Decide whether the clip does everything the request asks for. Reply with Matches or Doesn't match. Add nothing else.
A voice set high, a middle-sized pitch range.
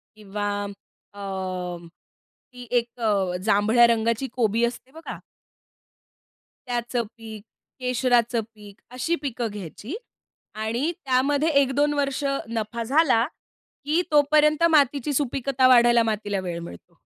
Matches